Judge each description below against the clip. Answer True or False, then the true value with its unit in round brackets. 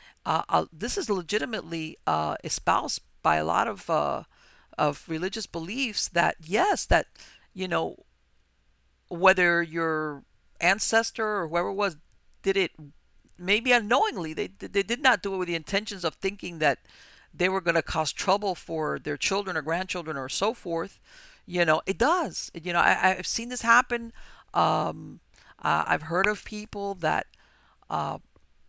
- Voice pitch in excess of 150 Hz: True (185 Hz)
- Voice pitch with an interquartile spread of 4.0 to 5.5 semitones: True (4.8 semitones)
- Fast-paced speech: False (155 wpm)